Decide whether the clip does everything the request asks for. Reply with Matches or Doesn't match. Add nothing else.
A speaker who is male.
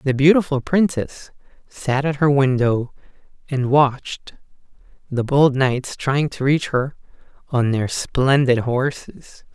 Matches